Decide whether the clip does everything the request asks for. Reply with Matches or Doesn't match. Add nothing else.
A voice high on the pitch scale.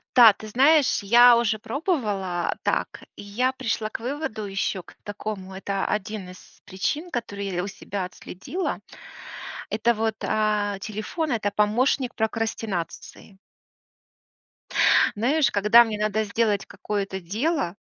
Matches